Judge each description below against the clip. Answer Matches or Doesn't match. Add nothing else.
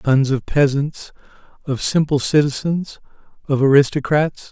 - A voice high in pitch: Doesn't match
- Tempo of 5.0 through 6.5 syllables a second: Doesn't match